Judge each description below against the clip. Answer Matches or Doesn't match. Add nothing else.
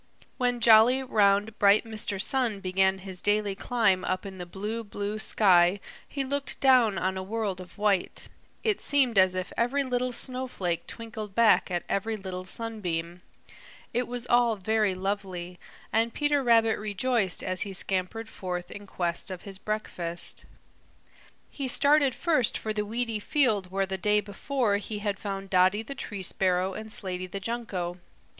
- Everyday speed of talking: Matches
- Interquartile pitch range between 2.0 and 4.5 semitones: Matches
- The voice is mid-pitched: Doesn't match